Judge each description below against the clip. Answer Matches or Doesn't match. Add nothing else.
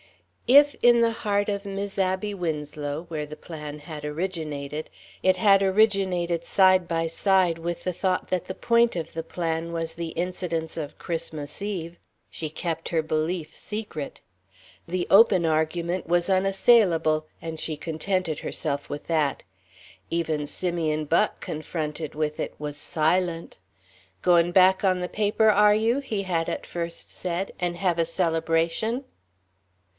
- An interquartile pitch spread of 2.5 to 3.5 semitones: Matches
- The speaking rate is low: Doesn't match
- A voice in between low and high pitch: Matches